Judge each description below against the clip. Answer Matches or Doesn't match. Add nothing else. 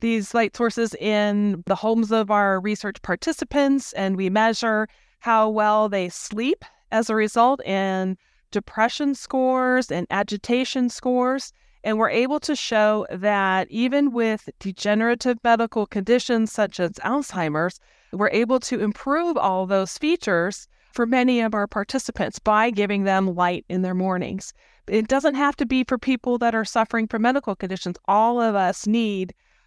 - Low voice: Doesn't match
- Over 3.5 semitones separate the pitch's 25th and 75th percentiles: Matches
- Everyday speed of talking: Matches